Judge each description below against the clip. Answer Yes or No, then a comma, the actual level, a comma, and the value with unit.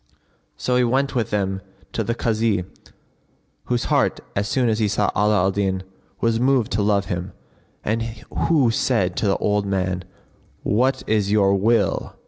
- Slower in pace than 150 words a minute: No, average, 165 wpm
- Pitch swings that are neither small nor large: Yes, average, 3.1 semitones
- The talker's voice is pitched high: No, low, 105 Hz